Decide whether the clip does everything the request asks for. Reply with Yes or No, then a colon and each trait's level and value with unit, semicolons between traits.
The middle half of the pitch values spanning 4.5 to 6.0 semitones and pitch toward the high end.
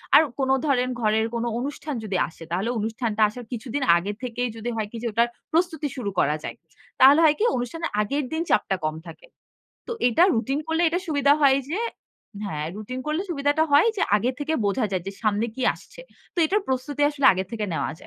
Yes: wide, 5.4 semitones; very high, 250 Hz